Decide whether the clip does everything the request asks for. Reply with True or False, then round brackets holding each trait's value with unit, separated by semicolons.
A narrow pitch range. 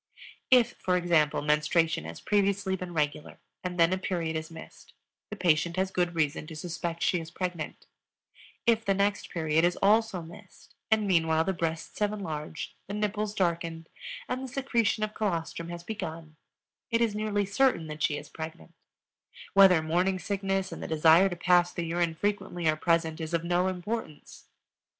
False (3.7 semitones)